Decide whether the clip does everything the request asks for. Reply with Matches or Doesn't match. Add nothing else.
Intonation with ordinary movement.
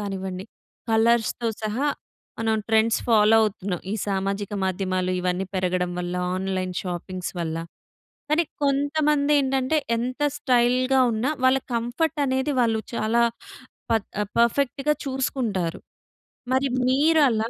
Doesn't match